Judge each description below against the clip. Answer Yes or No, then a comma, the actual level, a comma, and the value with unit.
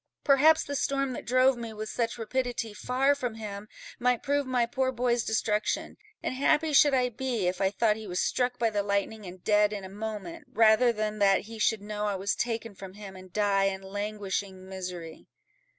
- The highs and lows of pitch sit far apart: No, average, 3.8 semitones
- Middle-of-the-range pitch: No, high, 220 Hz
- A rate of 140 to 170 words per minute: No, average, 200 wpm